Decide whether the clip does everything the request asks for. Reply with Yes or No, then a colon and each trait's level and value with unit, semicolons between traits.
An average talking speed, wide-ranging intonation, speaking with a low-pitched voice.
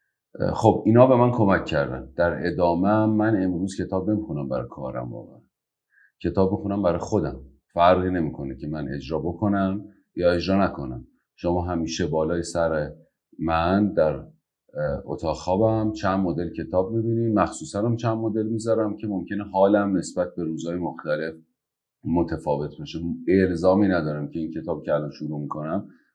No: average, 145 wpm; average, 4.1 semitones; very low, 90 Hz